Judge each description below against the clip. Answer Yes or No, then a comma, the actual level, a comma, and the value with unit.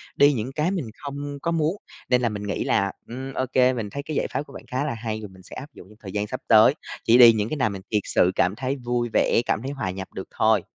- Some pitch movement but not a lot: Yes, average, 4.7 semitones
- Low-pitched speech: Yes, low, 120 Hz